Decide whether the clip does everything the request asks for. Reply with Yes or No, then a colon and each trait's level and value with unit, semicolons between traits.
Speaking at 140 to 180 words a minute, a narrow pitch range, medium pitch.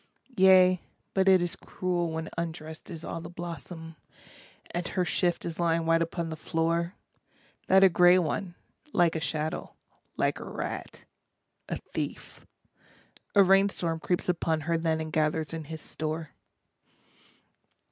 Yes: average, 145 wpm; narrow, 1.7 semitones; medium, 165 Hz